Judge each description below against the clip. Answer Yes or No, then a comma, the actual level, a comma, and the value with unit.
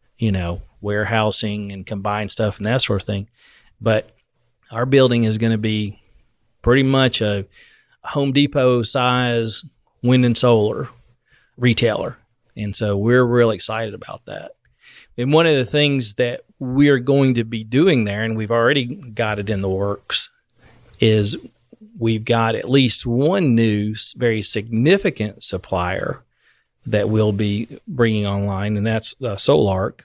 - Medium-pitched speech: No, low, 115 Hz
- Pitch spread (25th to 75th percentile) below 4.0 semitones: Yes, average, 3.1 semitones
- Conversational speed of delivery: Yes, average, 150 wpm